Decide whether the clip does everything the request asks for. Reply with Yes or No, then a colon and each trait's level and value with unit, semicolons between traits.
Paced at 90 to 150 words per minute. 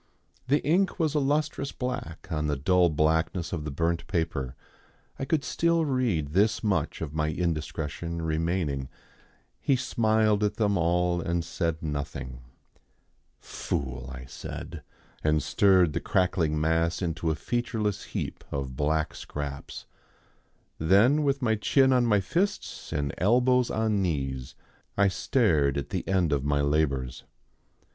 Yes: average, 140 wpm